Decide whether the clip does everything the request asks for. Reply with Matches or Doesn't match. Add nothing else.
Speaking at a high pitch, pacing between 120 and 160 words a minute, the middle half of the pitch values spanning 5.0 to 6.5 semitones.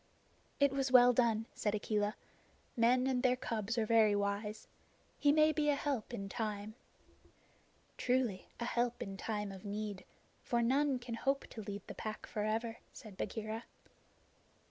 Doesn't match